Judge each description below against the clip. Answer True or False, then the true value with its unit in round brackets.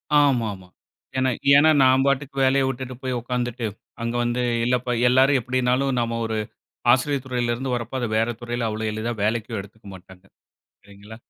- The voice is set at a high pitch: False (120 Hz)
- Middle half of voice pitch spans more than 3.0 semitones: False (2.6 semitones)